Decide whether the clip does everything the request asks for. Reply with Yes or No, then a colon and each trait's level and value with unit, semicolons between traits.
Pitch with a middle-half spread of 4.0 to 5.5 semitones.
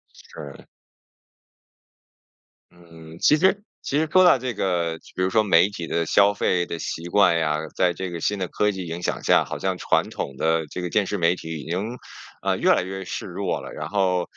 No: average, 3.5 semitones